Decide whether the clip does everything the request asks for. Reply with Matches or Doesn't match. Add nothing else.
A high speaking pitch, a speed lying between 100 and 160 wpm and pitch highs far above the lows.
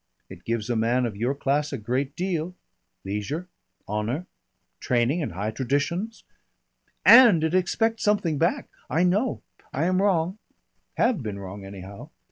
Doesn't match